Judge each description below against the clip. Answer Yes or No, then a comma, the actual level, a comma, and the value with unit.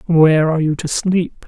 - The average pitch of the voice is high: No, medium, 165 Hz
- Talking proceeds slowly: No, fast, 205 wpm